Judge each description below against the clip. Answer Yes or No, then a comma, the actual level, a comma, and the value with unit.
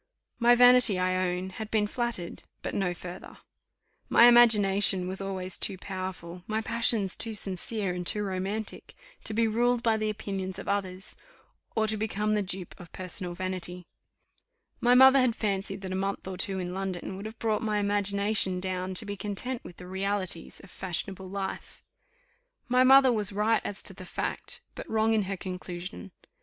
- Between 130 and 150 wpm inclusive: No, average, 175 wpm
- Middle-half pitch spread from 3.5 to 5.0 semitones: No, average, 2.7 semitones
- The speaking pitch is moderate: No, high, 195 Hz